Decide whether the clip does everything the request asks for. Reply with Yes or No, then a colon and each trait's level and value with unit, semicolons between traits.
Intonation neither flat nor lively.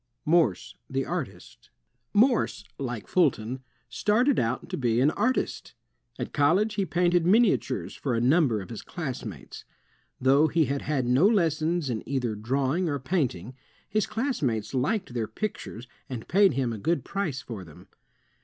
No: wide, 7.1 semitones